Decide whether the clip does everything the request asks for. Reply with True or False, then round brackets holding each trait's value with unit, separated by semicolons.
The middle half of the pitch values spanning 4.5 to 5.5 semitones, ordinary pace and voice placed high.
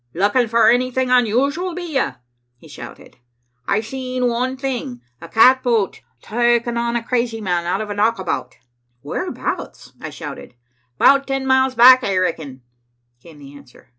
True (5.2 semitones; 150 wpm; 235 Hz)